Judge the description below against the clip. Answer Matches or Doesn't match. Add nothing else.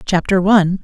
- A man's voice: Doesn't match